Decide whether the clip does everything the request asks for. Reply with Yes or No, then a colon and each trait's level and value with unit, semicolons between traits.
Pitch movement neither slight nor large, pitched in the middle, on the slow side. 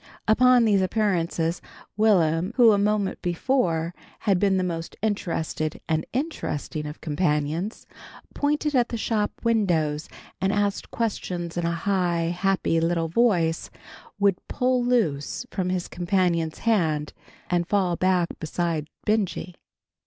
Yes: average, 4.3 semitones; medium, 180 Hz; slow, 130 wpm